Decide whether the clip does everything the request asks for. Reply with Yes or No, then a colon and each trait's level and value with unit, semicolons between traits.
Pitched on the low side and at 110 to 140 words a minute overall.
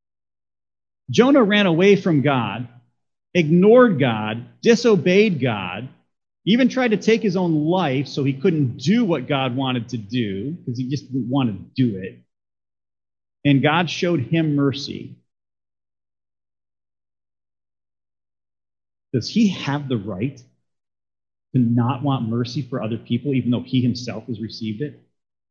Yes: low, 120 Hz; slow, 135 wpm